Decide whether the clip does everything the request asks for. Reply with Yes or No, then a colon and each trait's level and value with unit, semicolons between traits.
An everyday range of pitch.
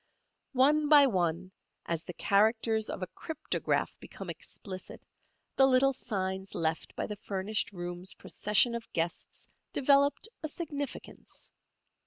No: wide, 6.5 semitones